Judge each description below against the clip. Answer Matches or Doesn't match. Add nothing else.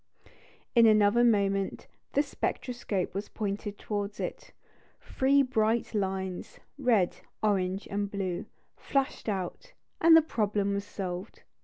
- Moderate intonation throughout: Matches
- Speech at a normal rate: Doesn't match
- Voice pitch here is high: Matches